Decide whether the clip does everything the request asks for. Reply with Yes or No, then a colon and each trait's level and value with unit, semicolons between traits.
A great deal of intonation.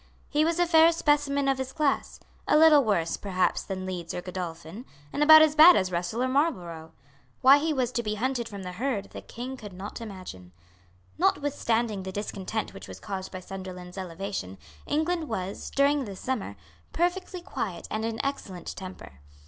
Yes: wide, 7.5 semitones